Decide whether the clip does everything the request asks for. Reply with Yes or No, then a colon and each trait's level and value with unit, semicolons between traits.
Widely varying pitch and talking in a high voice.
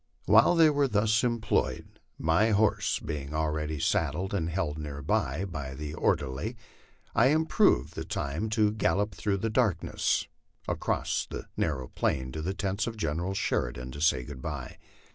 No: wide, 6.6 semitones; very low, 85 Hz